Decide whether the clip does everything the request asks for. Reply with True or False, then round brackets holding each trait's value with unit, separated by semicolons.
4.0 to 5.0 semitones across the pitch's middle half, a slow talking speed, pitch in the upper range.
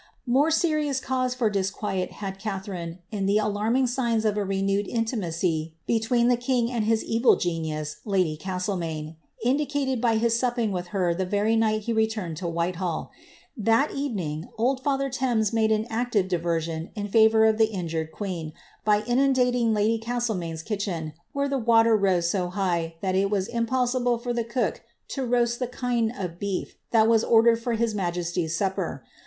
False (4.6 semitones; 175 wpm; 215 Hz)